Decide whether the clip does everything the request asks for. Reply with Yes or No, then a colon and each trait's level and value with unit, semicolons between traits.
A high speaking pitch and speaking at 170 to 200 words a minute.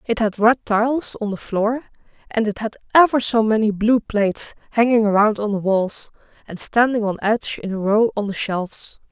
Yes: high, 220 Hz; average, 195 wpm